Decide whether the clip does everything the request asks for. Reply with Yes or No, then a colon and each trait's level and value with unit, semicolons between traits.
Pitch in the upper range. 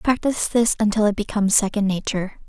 Yes: high, 210 Hz